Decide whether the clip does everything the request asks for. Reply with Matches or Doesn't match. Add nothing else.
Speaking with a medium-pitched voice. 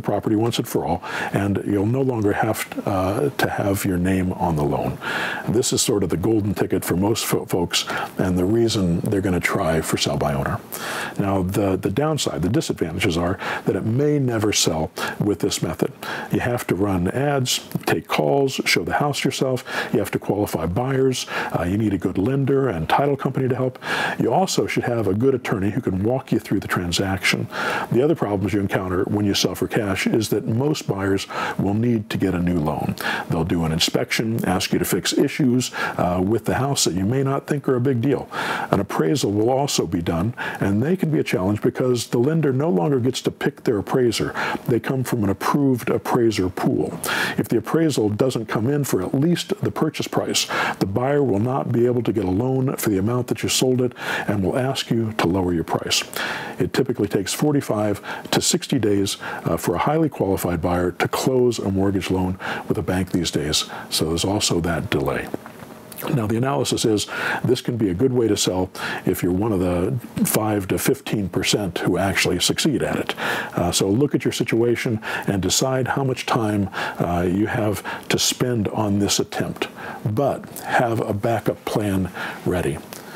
Doesn't match